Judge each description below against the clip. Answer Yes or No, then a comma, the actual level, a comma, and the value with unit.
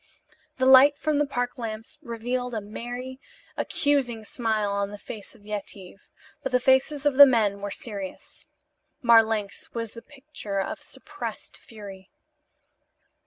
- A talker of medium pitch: No, high, 230 Hz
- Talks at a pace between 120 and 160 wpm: Yes, average, 140 wpm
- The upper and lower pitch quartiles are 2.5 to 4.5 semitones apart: Yes, average, 4.0 semitones